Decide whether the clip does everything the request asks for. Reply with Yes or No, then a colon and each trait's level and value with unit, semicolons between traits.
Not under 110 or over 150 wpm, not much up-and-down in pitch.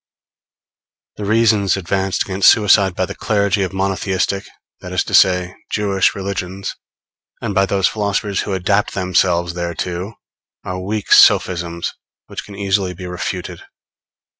Yes: average, 140 wpm; narrow, 1.7 semitones